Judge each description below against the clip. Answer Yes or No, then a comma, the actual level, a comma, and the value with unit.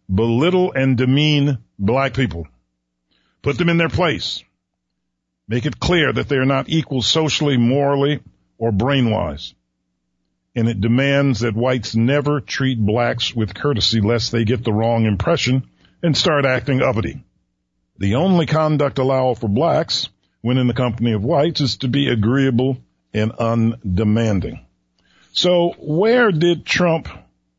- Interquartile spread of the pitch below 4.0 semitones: No, average, 5.2 semitones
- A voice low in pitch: Yes, low, 120 Hz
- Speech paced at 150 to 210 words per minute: No, average, 140 wpm